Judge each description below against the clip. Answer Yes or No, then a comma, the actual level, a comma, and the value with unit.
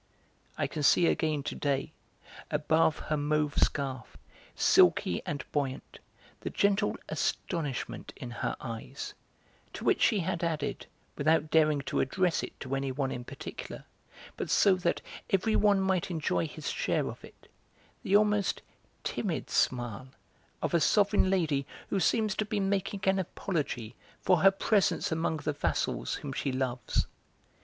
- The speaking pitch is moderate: Yes, medium, 155 Hz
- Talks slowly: No, average, 145 wpm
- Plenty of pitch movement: Yes, wide, 5.8 semitones